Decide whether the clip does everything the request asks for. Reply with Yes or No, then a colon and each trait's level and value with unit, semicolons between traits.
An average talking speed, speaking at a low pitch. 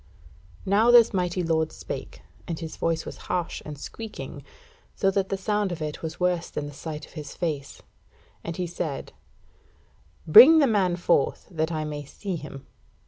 No: average, 175 wpm; medium, 170 Hz